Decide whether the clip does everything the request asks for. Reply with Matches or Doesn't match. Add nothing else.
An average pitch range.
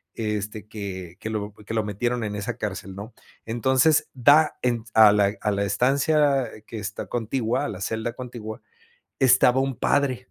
Matches